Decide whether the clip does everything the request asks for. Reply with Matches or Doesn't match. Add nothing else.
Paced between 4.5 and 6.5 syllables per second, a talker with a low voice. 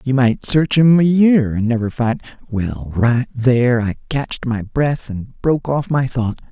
Doesn't match